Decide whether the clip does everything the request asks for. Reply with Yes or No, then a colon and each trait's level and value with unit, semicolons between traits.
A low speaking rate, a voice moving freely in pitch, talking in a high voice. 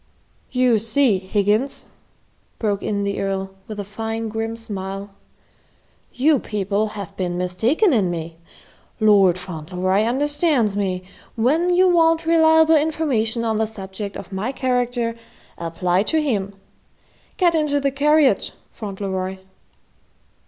Yes: slow, 125 wpm; wide, 6.2 semitones; high, 220 Hz